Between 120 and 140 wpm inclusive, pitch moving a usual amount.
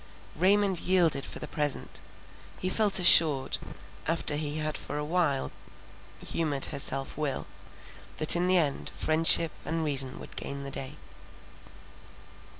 Yes: slow, 135 wpm; average, 3.6 semitones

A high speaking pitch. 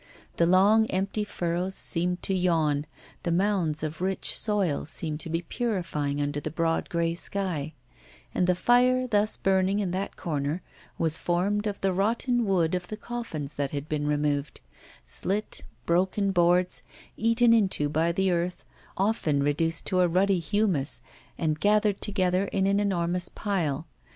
No: medium, 180 Hz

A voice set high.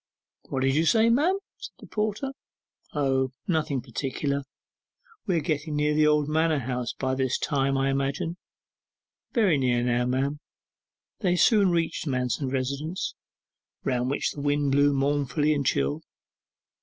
No: medium, 145 Hz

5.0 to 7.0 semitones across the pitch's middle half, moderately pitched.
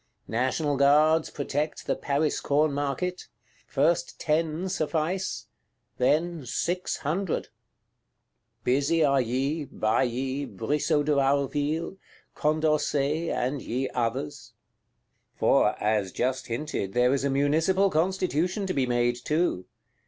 No: average, 3.5 semitones; medium, 145 Hz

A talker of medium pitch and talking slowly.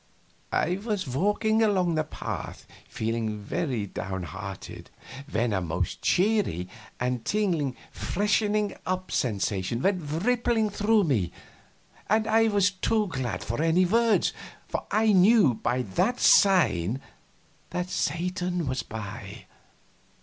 Yes: medium, 175 Hz; slow, 120 wpm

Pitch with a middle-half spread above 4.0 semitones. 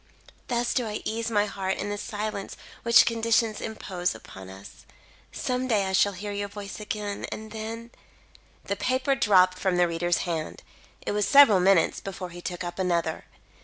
No: average, 3.6 semitones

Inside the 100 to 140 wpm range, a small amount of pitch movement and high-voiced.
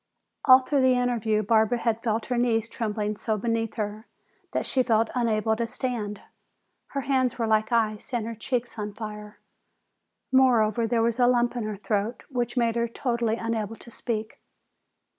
No: average, 175 wpm; narrow, 2.0 semitones; high, 230 Hz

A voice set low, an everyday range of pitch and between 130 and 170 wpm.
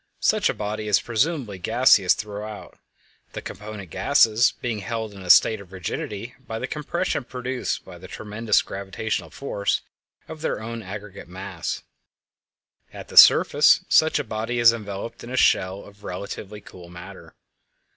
Yes: low, 105 Hz; average, 3.1 semitones; average, 155 wpm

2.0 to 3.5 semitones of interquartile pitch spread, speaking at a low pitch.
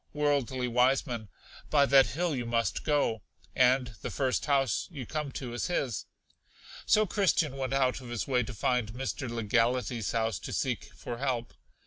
Yes: average, 2.8 semitones; low, 130 Hz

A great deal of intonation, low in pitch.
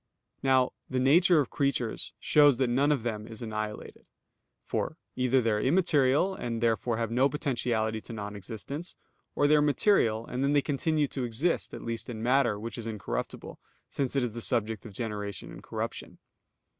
No: average, 4.1 semitones; low, 120 Hz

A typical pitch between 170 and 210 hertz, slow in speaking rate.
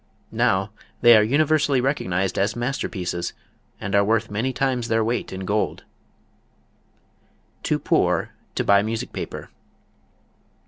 No: low, 110 Hz; slow, 125 wpm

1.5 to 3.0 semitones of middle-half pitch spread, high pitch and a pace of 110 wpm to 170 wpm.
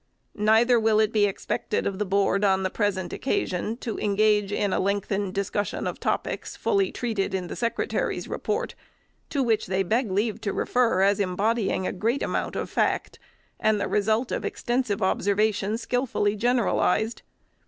Yes: narrow, 2.5 semitones; high, 210 Hz; average, 165 wpm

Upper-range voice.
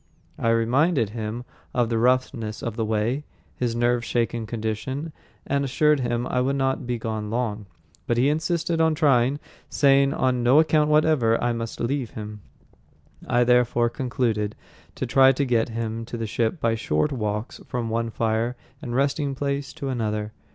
No: low, 120 Hz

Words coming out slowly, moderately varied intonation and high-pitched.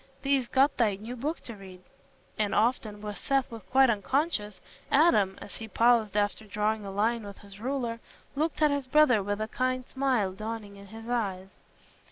No: average, 185 wpm; average, 4.0 semitones; high, 225 Hz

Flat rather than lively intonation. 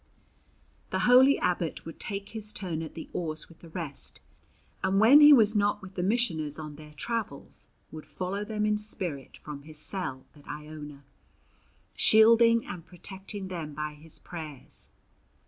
No: wide, 5.5 semitones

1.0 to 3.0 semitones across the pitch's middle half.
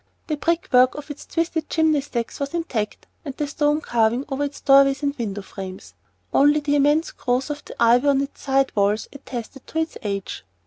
No: average, 3.6 semitones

